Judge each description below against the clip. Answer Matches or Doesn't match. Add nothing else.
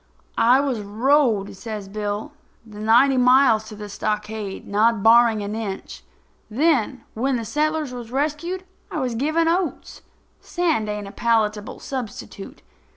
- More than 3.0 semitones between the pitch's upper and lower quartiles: Matches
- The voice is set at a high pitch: Matches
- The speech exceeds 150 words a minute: Doesn't match